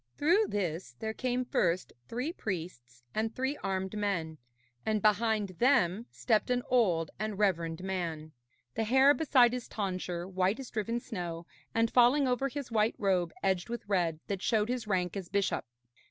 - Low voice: No, high, 210 Hz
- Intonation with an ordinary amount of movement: Yes, average, 5.0 semitones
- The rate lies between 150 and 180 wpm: Yes, average, 165 wpm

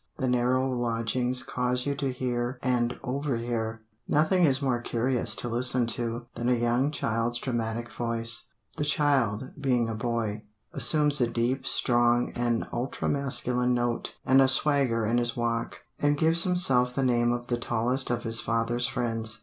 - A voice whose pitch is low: Yes, low, 120 Hz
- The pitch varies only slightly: Yes, narrow, 2.0 semitones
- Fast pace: No, average, 165 wpm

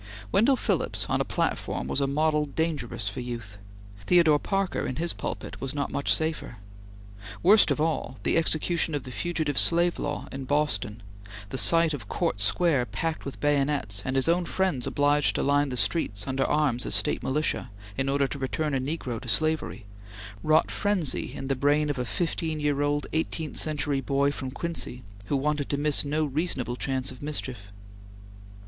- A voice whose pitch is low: No, medium, 145 Hz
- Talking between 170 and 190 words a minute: Yes, average, 180 wpm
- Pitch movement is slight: No, average, 3.3 semitones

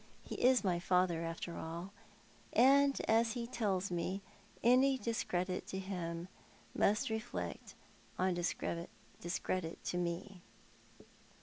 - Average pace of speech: No, slow, 105 wpm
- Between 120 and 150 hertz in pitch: No, medium, 185 Hz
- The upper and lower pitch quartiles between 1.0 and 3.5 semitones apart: No, average, 4.6 semitones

